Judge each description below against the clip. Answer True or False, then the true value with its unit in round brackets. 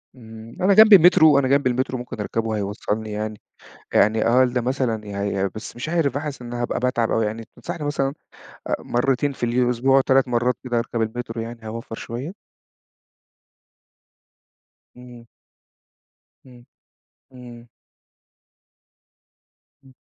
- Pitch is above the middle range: False (120 Hz)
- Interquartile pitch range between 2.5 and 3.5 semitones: True (3.0 semitones)